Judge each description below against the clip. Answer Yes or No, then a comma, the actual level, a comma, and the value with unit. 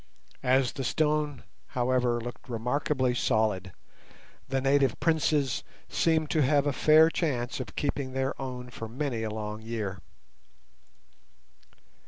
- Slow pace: Yes, slow, 125 wpm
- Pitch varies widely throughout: No, average, 3.7 semitones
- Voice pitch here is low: Yes, low, 130 Hz